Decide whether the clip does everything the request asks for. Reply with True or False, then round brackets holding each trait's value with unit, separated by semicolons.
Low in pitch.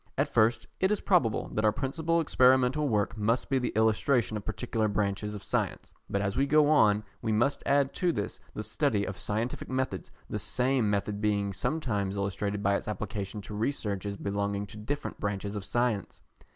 True (110 Hz)